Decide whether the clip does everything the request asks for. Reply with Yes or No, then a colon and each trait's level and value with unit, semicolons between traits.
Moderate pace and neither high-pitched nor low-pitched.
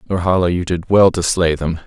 No: average, 195 wpm; very low, 90 Hz